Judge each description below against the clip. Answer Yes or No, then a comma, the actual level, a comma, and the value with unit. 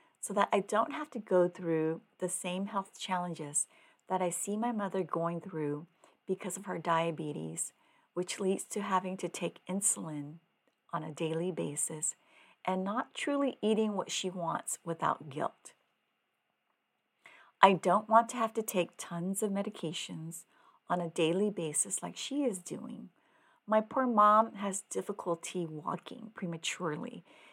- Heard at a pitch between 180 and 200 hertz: Yes, medium, 185 Hz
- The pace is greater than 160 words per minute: No, average, 150 wpm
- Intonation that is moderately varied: Yes, average, 3.9 semitones